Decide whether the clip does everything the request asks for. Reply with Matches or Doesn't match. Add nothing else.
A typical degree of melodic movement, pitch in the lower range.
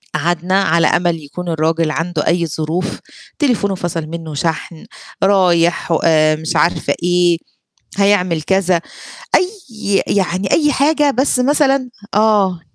Doesn't match